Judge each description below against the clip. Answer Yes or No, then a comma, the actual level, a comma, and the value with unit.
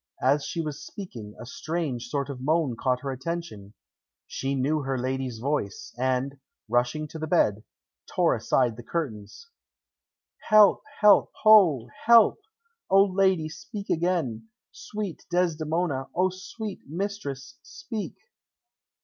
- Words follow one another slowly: Yes, slow, 125 wpm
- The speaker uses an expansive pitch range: Yes, wide, 6.2 semitones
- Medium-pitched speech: Yes, medium, 155 Hz